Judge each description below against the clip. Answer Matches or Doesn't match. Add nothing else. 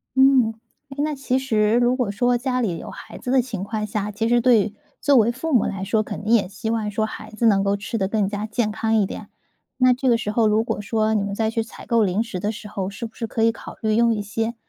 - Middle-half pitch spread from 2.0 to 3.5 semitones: Matches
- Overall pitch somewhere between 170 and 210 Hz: Doesn't match